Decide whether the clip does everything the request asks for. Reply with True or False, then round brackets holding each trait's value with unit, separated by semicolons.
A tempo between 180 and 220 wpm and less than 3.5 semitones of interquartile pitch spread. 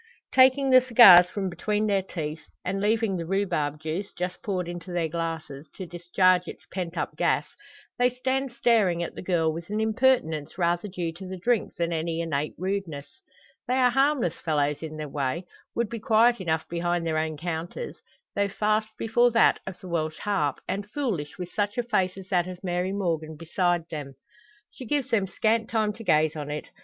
False (190 wpm; 4.9 semitones)